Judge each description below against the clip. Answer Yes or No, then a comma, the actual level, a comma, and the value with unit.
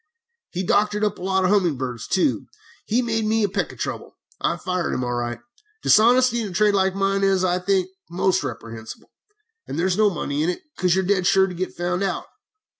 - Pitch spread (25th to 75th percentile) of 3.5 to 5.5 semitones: No, average, 2.7 semitones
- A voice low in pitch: No, high, 190 Hz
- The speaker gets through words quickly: Yes, fast, 225 wpm